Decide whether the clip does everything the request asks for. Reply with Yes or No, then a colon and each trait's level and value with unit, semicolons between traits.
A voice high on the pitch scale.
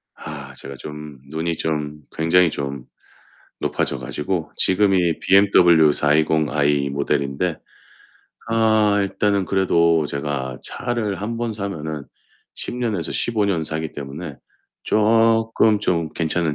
No: very low, 80 Hz